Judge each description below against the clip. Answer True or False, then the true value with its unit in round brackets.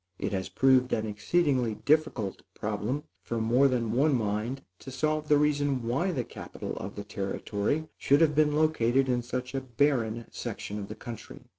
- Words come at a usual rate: True (175 wpm)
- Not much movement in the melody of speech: False (4.7 semitones)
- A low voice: True (125 Hz)